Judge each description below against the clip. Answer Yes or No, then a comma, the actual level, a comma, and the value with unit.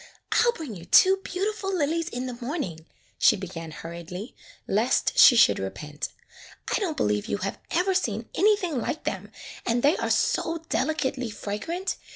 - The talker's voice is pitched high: Yes, very high, 255 Hz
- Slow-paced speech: No, average, 165 wpm